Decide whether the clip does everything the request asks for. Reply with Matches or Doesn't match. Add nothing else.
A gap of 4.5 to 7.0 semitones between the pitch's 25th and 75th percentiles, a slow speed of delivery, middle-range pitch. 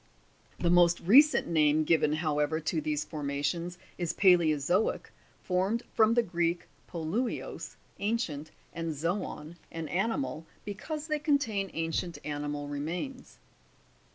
Matches